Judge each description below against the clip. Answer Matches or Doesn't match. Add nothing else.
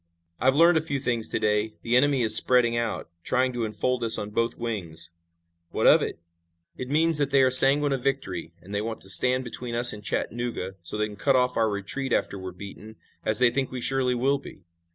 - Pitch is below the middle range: Matches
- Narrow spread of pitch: Doesn't match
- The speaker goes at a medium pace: Doesn't match